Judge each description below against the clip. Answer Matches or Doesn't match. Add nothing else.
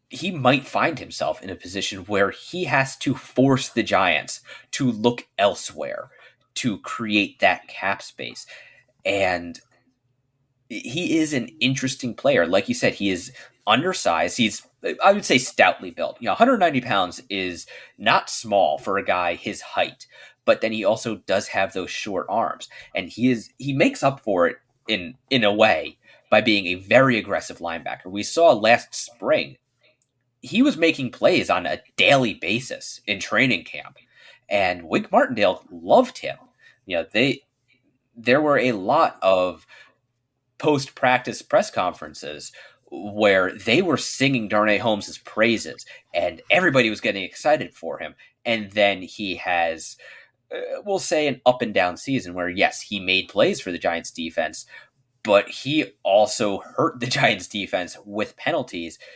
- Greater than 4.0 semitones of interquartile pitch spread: Matches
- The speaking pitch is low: Matches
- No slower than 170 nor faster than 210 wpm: Doesn't match